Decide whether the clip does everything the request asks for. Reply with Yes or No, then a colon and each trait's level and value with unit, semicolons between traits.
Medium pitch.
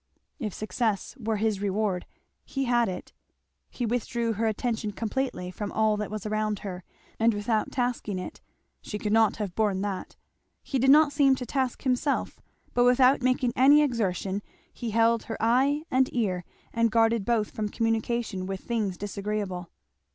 No: high, 225 Hz